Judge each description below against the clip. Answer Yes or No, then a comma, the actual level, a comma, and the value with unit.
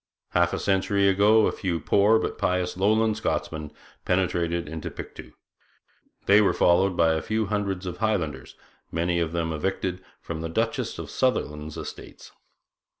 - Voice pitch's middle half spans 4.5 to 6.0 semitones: No, average, 3.4 semitones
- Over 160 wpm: No, average, 150 wpm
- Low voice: Yes, very low, 90 Hz